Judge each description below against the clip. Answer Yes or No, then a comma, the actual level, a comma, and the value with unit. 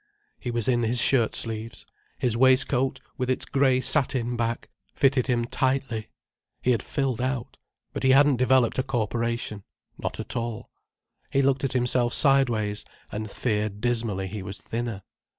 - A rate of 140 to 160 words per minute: Yes, average, 150 wpm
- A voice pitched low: Yes, low, 120 Hz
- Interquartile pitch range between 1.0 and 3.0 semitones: Yes, narrow, 2.5 semitones